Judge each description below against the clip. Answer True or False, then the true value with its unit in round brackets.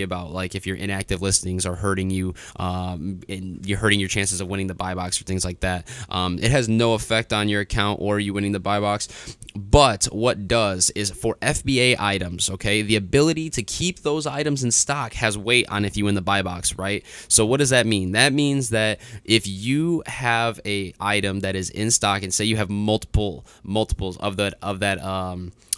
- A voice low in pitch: True (100 Hz)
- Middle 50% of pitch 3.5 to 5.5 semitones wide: False (3.1 semitones)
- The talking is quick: True (215 wpm)